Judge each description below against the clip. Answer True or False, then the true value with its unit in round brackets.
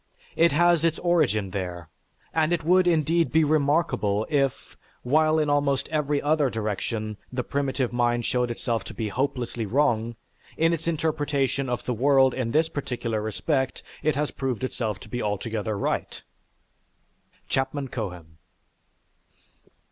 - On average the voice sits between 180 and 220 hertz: False (135 Hz)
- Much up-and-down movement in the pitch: False (5.0 semitones)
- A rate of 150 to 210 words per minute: False (140 wpm)